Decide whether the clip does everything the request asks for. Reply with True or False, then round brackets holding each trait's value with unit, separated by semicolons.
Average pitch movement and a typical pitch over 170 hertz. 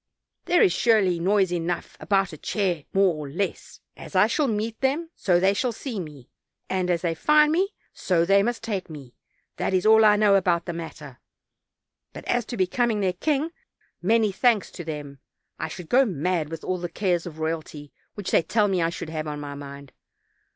True (4.8 semitones; 185 Hz)